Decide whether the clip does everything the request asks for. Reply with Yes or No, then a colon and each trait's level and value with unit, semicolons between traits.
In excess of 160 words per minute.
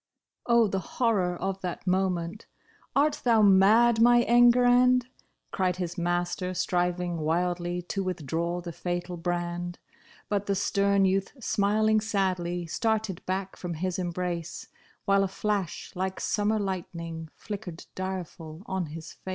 No: average, 145 wpm